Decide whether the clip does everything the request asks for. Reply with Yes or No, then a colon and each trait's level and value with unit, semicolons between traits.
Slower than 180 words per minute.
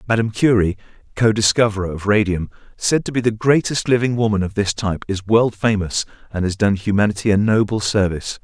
No: average, 185 wpm